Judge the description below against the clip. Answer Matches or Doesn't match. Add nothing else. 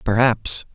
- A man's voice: Matches